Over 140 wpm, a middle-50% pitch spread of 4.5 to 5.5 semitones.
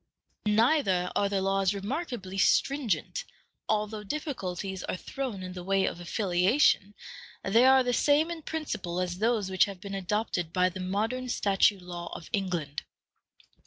Yes: average, 150 wpm; average, 4.8 semitones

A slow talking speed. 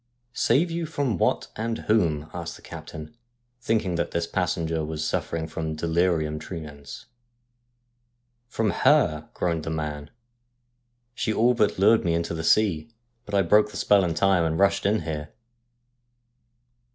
No: average, 165 wpm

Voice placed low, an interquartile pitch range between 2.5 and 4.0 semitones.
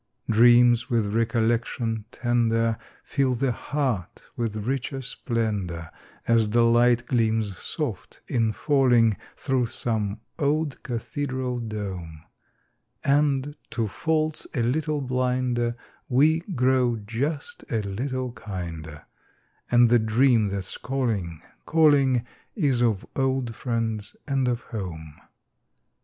Yes: low, 120 Hz; average, 3.1 semitones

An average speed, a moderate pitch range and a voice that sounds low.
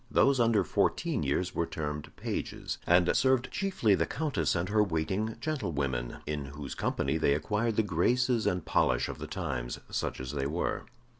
No: average, 170 wpm; wide, 7.5 semitones; very low, 90 Hz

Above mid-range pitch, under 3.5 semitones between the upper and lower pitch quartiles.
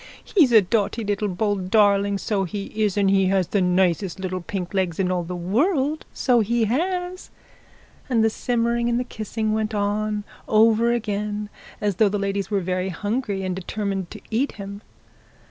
Yes: high, 205 Hz; average, 2.8 semitones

